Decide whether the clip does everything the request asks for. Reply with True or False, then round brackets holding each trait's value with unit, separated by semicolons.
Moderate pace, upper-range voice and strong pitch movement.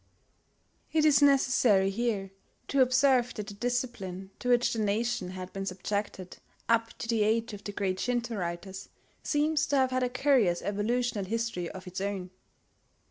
False (165 wpm; 225 Hz; 4.3 semitones)